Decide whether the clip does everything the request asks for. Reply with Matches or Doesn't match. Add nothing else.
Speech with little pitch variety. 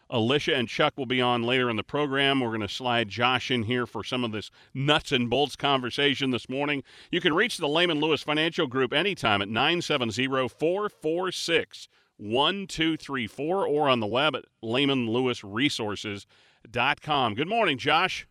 Doesn't match